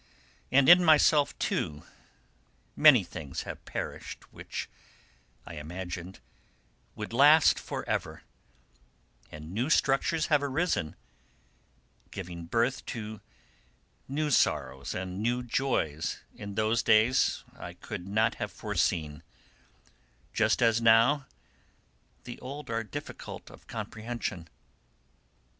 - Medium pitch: No, low, 115 Hz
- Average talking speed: No, slow, 110 wpm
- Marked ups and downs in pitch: Yes, wide, 7.1 semitones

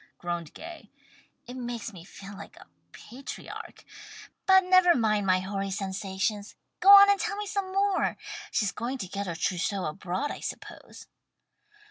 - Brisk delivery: No, average, 155 wpm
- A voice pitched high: Yes, high, 215 Hz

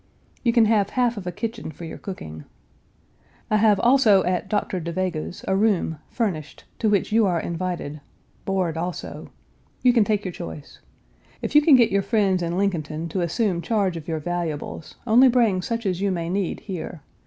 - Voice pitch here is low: No, high, 190 Hz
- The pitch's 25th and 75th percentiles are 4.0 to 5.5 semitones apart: Yes, average, 4.4 semitones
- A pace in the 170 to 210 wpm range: Yes, average, 190 wpm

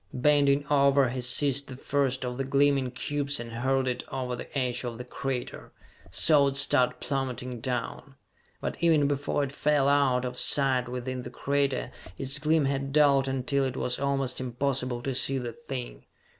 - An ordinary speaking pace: Yes, average, 175 wpm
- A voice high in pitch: No, low, 135 Hz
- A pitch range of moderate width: No, narrow, 1.9 semitones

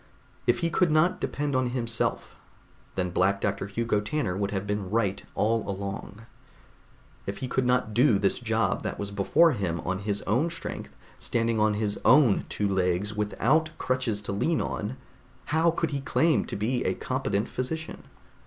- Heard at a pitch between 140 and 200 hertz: No, low, 110 Hz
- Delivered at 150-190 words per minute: Yes, average, 170 wpm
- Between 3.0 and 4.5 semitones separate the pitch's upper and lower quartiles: No, average, 4.9 semitones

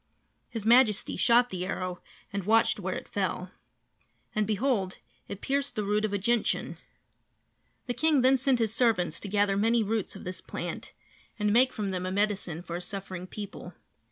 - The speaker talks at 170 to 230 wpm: Yes, average, 180 wpm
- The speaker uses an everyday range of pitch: Yes, average, 3.7 semitones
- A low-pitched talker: No, high, 210 Hz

